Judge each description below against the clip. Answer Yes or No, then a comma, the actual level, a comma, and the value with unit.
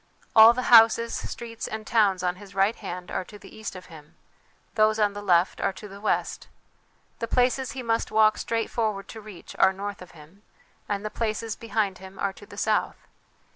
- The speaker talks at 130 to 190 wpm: No, fast, 205 wpm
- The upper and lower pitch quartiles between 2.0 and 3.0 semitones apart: Yes, average, 2.7 semitones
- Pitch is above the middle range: Yes, high, 210 Hz